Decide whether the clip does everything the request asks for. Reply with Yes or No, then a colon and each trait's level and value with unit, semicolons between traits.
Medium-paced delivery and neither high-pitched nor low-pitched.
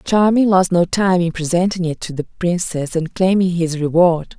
Yes: average, 190 wpm; medium, 175 Hz